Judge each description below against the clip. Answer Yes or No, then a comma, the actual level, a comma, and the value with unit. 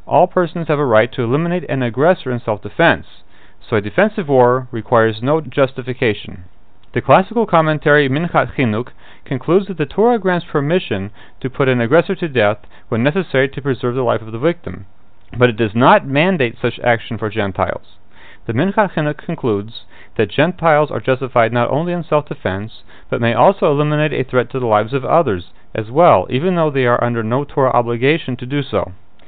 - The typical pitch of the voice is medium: No, low, 130 Hz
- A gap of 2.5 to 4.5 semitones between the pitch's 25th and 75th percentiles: No, wide, 5.6 semitones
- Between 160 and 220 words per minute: Yes, average, 185 wpm